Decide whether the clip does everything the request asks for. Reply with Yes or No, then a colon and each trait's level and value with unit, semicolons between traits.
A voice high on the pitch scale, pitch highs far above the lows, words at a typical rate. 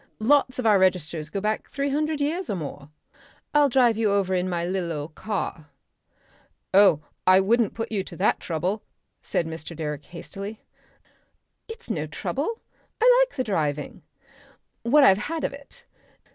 Yes: high, 200 Hz; wide, 7.8 semitones; average, 165 wpm